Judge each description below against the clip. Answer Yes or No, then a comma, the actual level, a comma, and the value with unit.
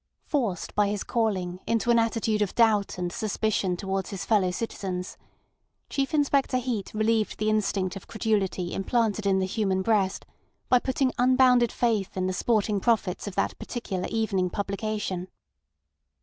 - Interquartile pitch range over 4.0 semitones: No, average, 3.2 semitones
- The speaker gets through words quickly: No, average, 150 wpm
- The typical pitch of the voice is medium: No, high, 210 Hz